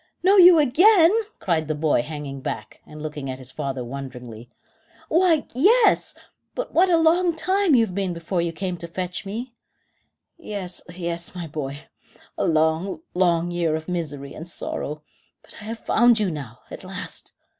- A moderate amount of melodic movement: No, wide, 8.5 semitones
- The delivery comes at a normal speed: Yes, average, 170 wpm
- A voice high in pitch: No, medium, 175 Hz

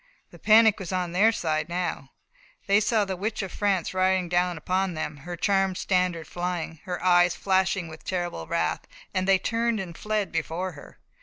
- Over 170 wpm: Yes, average, 180 wpm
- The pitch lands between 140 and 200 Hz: Yes, medium, 185 Hz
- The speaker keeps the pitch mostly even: Yes, narrow, 2.1 semitones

